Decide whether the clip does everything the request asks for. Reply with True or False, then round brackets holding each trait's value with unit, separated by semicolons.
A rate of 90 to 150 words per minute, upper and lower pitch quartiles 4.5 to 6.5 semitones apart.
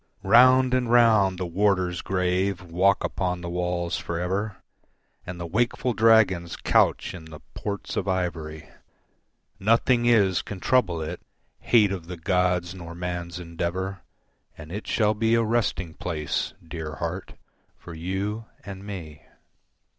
False (140 wpm; 3.3 semitones)